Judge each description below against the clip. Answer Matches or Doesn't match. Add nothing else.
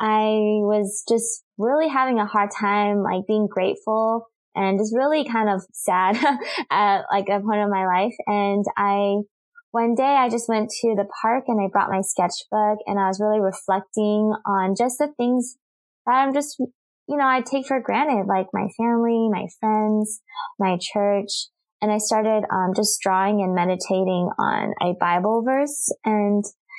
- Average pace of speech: Matches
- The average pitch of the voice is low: Doesn't match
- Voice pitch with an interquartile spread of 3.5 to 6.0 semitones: Doesn't match